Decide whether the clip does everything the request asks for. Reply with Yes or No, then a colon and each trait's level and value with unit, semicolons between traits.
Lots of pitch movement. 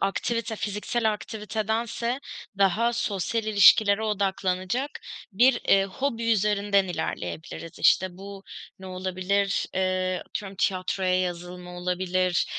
No: average, 2.9 semitones